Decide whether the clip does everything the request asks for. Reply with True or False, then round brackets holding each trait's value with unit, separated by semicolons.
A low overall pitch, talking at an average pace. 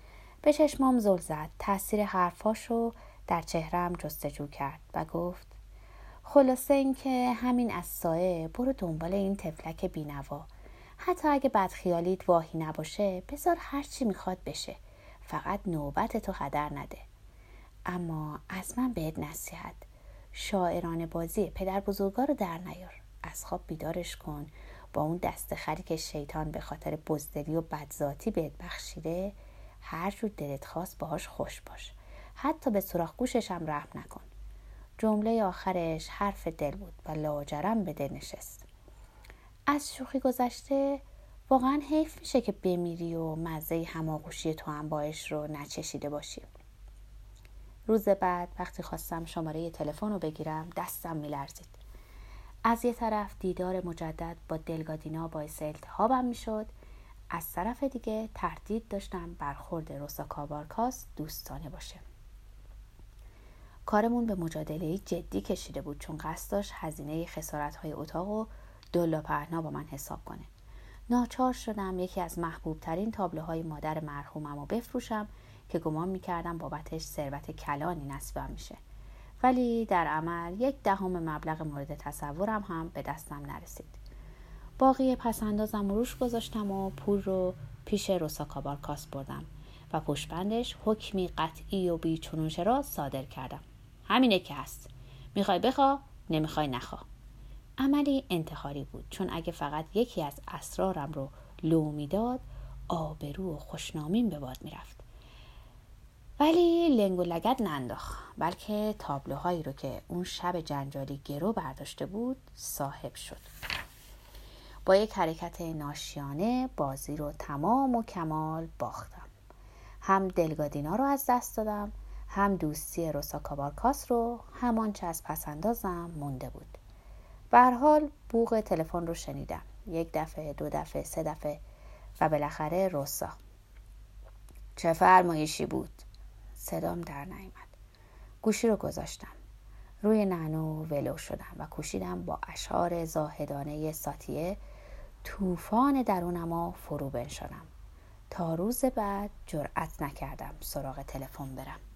False (165 Hz; 130 wpm)